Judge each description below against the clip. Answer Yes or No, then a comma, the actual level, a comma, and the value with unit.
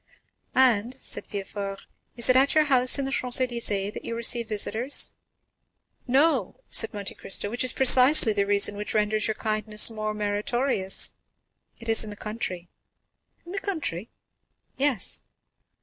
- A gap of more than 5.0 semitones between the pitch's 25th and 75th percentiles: No, average, 3.7 semitones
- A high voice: Yes, high, 225 Hz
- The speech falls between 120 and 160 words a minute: Yes, average, 150 wpm